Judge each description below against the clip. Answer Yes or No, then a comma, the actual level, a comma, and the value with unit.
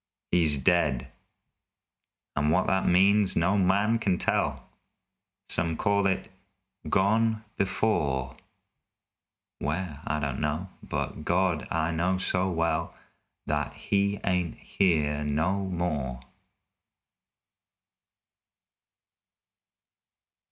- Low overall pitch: Yes, very low, 90 Hz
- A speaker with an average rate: No, slow, 90 wpm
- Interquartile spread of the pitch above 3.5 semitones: Yes, average, 4.2 semitones